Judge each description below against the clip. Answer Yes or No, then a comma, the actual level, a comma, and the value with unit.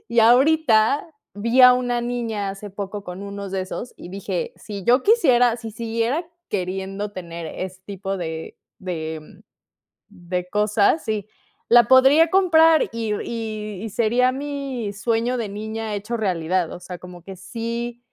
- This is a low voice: No, high, 215 Hz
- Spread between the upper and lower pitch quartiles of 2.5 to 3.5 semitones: No, average, 4.0 semitones